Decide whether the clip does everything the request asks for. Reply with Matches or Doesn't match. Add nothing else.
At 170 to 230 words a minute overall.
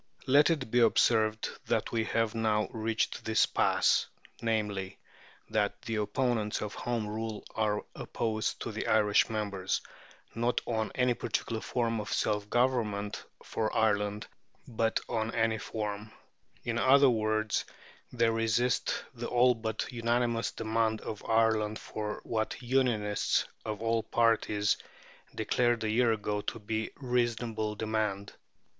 Doesn't match